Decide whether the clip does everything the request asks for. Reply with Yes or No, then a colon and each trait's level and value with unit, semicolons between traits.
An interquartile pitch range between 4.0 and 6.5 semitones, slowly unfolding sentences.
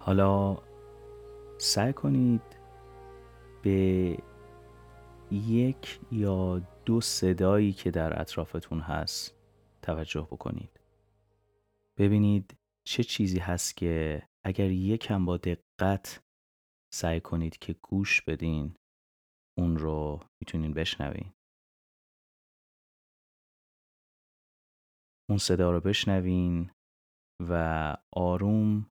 Yes: average, 4.4 semitones; slow, 80 wpm